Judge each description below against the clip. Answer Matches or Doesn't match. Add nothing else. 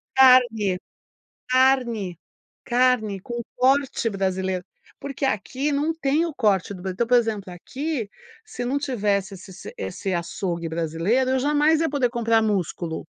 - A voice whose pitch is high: Matches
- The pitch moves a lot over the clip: Matches